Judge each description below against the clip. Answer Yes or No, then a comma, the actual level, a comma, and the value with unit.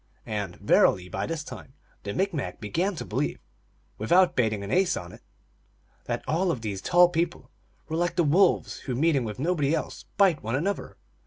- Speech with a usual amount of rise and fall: No, wide, 8.2 semitones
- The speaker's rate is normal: Yes, average, 180 wpm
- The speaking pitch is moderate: Yes, medium, 155 Hz